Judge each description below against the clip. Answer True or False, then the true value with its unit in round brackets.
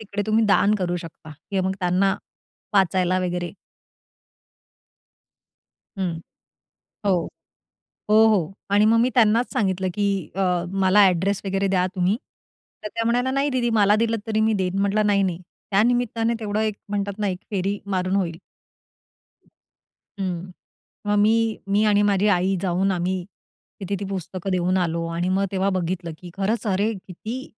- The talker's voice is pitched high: True (195 Hz)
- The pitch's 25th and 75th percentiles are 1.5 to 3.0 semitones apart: True (2.4 semitones)